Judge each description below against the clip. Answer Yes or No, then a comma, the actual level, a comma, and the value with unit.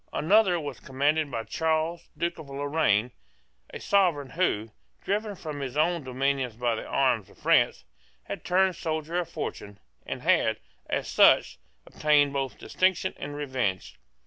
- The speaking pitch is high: No, medium, 145 Hz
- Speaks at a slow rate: No, average, 145 wpm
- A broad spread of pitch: No, average, 4.5 semitones